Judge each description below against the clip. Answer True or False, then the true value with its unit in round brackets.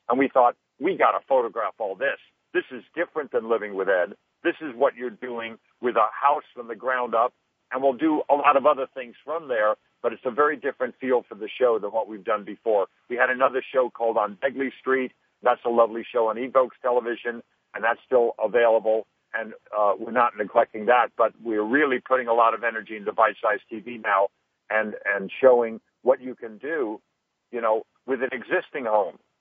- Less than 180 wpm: False (205 wpm)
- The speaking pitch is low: True (125 Hz)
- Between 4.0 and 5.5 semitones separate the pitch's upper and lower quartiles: False (2.8 semitones)